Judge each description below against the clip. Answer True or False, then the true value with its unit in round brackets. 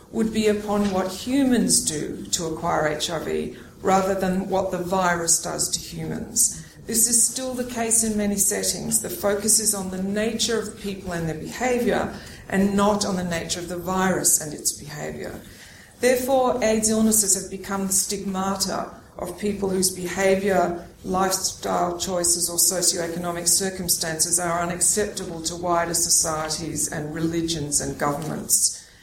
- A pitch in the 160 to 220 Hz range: True (190 Hz)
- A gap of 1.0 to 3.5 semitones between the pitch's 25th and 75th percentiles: True (3.0 semitones)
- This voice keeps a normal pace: True (150 wpm)